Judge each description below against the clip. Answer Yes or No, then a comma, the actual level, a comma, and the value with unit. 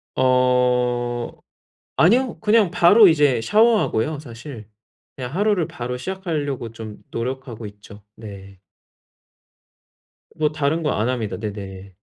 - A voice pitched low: Yes, low, 125 Hz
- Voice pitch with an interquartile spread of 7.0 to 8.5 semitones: No, wide, 6.1 semitones